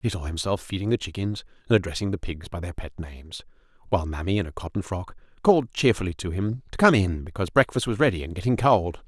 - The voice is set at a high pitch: No, low, 100 Hz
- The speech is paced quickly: Yes, fast, 225 wpm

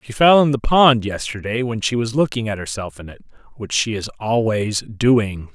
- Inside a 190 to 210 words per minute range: Yes, fast, 205 wpm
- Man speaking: Yes, male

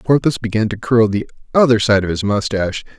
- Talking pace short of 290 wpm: Yes, average, 200 wpm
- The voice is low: Yes, low, 110 Hz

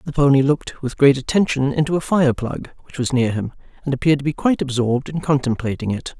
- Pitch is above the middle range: No, medium, 140 Hz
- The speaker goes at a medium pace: No, fast, 225 wpm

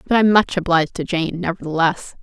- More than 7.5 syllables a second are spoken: No, 6.1 syllables/s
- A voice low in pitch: No, medium, 175 Hz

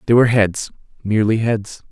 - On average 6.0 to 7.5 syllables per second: No, 5.8 syllables/s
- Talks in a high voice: No, low, 110 Hz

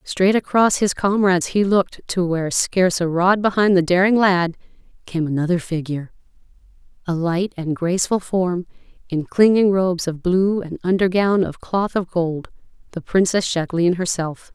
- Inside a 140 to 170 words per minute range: Yes, average, 155 wpm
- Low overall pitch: No, medium, 180 Hz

